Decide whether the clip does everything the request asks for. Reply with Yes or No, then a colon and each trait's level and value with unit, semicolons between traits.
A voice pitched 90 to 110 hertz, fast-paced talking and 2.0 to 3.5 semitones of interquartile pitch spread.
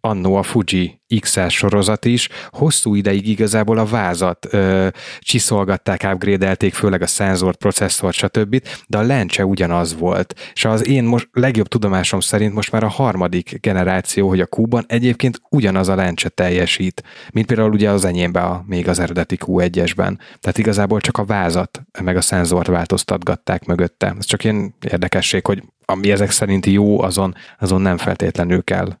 Yes: low, 100 Hz; fast, 160 wpm; average, 2.9 semitones